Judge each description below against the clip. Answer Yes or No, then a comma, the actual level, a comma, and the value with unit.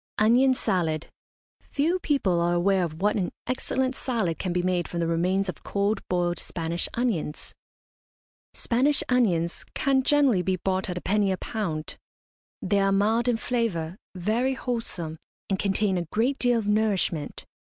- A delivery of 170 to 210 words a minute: No, average, 160 wpm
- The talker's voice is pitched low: No, high, 195 Hz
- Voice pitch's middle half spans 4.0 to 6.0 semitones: Yes, wide, 5.4 semitones